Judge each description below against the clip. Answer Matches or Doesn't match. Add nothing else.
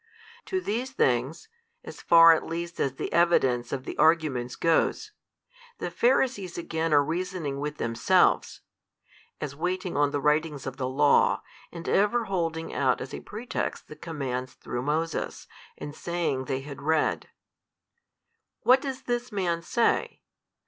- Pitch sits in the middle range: Matches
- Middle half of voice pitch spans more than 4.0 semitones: Matches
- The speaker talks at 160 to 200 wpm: Doesn't match